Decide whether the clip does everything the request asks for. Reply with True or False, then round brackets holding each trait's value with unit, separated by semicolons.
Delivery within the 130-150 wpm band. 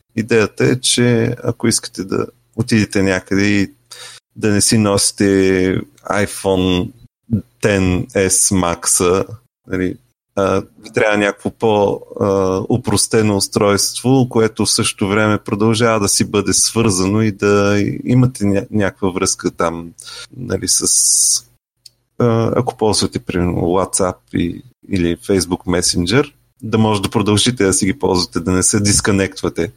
False (120 wpm)